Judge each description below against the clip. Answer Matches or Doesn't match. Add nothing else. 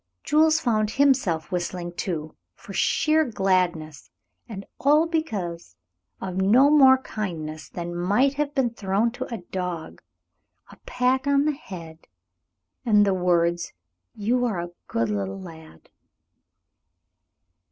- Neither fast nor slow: Doesn't match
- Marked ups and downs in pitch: Matches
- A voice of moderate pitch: Doesn't match